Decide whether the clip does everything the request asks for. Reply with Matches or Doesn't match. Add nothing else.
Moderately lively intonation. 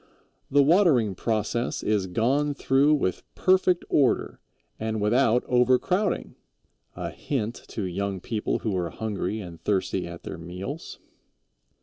Doesn't match